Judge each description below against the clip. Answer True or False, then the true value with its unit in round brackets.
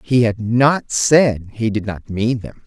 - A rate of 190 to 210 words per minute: True (205 wpm)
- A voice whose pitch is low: True (115 Hz)